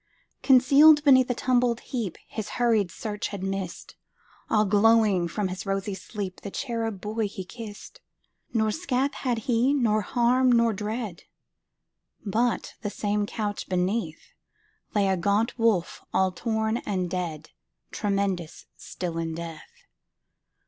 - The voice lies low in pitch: No, high, 210 Hz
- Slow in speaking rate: Yes, slow, 115 wpm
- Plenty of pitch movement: No, average, 3.8 semitones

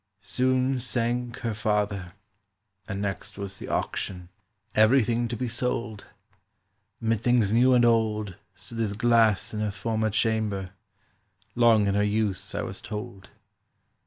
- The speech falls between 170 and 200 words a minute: No, slow, 135 wpm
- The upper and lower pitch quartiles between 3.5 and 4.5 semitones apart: No, narrow, 2.6 semitones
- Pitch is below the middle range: Yes, low, 110 Hz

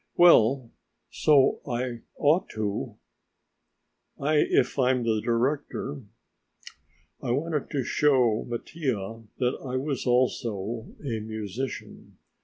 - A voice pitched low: Yes, low, 125 Hz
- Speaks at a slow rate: Yes, slow, 95 wpm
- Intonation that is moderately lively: Yes, average, 3.6 semitones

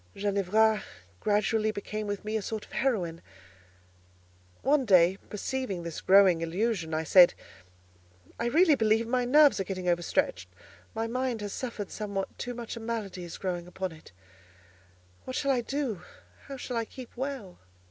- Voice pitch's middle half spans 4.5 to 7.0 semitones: Yes, average, 5.2 semitones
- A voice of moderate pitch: No, high, 210 Hz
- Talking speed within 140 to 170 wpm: Yes, average, 155 wpm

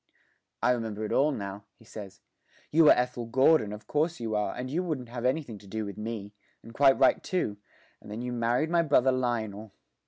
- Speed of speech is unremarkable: No, fast, 210 wpm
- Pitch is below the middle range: Yes, low, 120 Hz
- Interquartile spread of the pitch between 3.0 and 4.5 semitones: Yes, average, 4.1 semitones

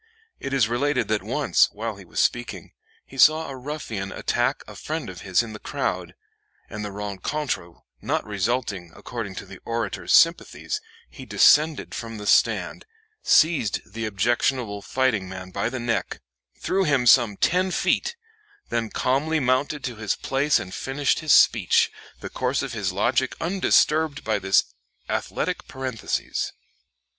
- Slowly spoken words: No, average, 150 wpm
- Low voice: Yes, low, 120 Hz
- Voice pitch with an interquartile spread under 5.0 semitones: No, wide, 5.4 semitones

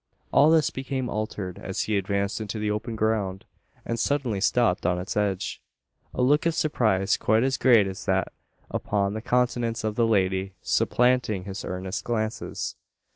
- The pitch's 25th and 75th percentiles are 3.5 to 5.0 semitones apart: Yes, average, 4.1 semitones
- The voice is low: Yes, low, 110 Hz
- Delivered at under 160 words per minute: No, average, 165 wpm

